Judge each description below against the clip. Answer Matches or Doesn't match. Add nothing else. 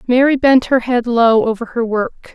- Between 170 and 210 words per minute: Matches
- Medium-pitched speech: Doesn't match